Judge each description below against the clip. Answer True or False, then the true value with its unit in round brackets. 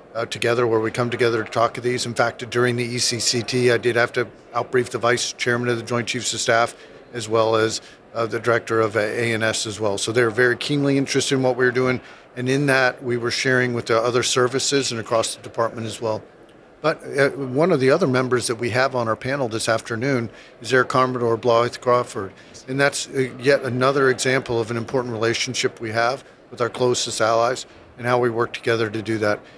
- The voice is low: True (120 Hz)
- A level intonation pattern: True (1.7 semitones)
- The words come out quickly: True (220 wpm)